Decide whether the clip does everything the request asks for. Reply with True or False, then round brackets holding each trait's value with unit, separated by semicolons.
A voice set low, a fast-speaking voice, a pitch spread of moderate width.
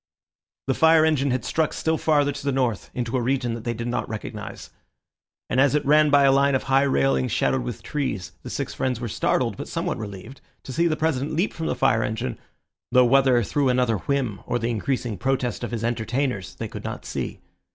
True (130 Hz; 215 wpm; 3.4 semitones)